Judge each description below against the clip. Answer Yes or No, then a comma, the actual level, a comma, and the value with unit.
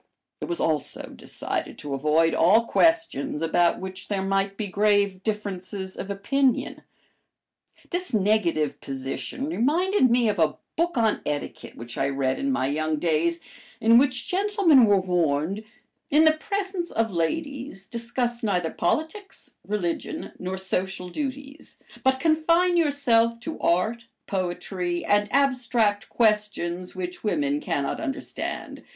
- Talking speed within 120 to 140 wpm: Yes, slow, 135 wpm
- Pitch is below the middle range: No, high, 205 Hz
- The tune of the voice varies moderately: No, wide, 7.7 semitones